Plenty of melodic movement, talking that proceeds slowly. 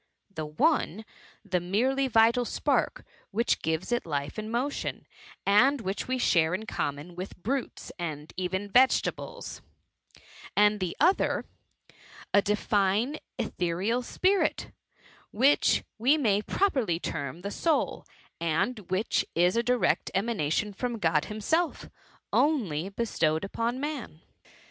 Yes: wide, 6.0 semitones; slow, 125 wpm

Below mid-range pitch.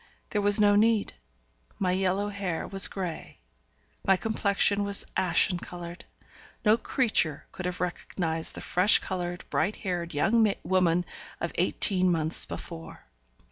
No: medium, 185 Hz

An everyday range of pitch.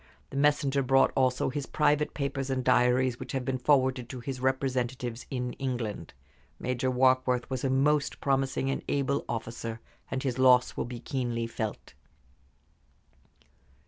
No: narrow, 1.5 semitones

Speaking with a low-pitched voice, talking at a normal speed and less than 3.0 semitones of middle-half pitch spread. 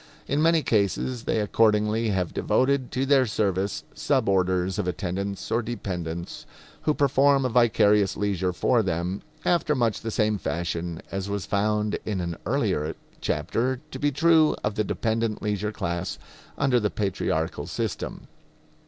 No: low, 105 Hz; average, 150 wpm; average, 4.6 semitones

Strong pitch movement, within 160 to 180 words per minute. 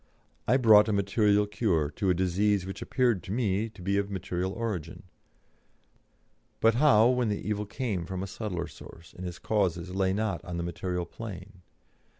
No: average, 3.0 semitones; average, 175 wpm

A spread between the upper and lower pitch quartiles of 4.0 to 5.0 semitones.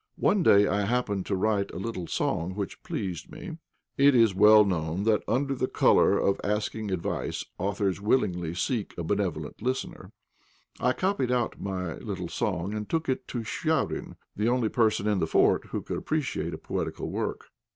Yes: average, 4.5 semitones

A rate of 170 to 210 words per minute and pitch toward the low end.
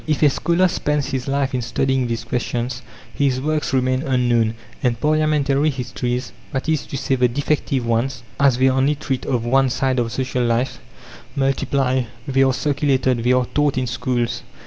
Yes: average, 175 wpm; low, 130 Hz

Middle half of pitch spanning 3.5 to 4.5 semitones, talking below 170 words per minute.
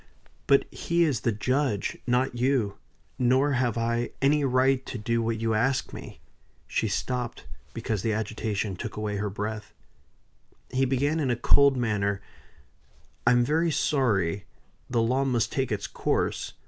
Yes: average, 3.8 semitones; average, 155 wpm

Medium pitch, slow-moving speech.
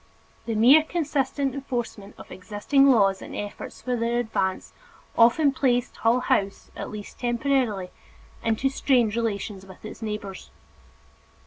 No: high, 235 Hz; slow, 130 wpm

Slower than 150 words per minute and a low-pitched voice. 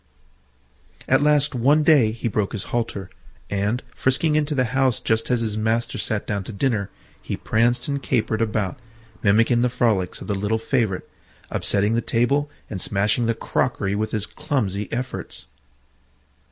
No: average, 160 wpm; low, 115 Hz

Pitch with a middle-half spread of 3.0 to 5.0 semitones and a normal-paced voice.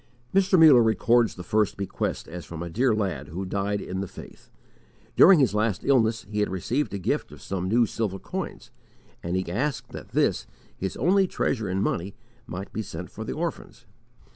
Yes: average, 4.4 semitones; average, 190 wpm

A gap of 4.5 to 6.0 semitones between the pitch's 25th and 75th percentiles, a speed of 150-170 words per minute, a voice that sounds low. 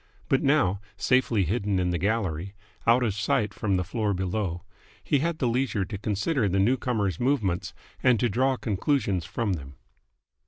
Yes: average, 4.8 semitones; average, 165 wpm; low, 105 Hz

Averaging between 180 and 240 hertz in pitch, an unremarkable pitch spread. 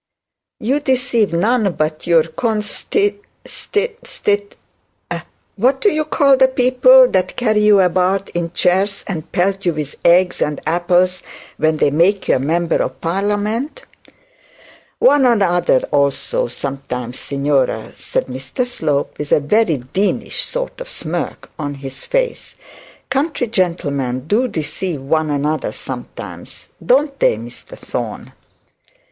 No: medium, 185 Hz; wide, 8.4 semitones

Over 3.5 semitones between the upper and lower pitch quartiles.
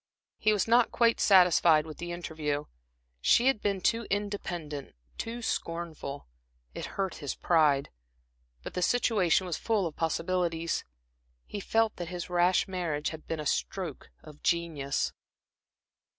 Yes: average, 4.2 semitones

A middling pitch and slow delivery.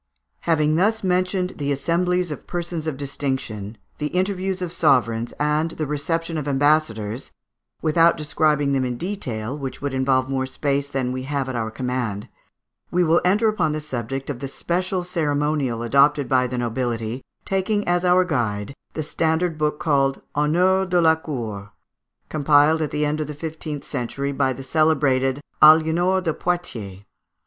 No: medium, 150 Hz; average, 165 wpm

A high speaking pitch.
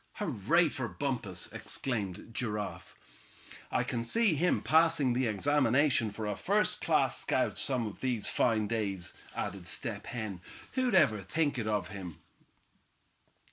No: low, 115 Hz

